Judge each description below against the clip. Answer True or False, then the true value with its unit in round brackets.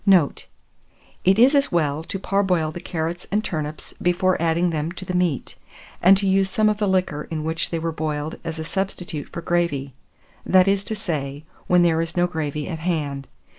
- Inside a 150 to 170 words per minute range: False (200 wpm)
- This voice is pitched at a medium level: True (170 Hz)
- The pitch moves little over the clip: False (3.2 semitones)